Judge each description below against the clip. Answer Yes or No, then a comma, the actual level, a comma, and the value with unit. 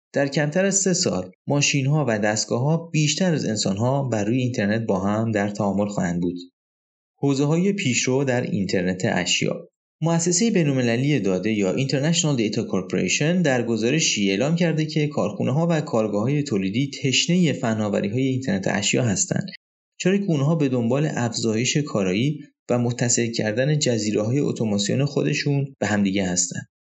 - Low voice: Yes, low, 130 Hz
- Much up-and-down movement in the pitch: Yes, wide, 6.0 semitones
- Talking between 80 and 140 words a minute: No, fast, 155 wpm